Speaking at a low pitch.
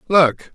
No: medium, 165 Hz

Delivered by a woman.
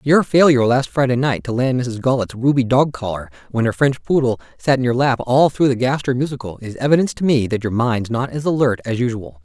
No: male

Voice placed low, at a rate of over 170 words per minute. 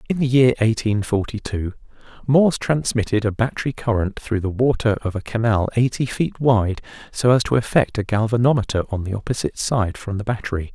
Yes: low, 115 Hz; average, 185 wpm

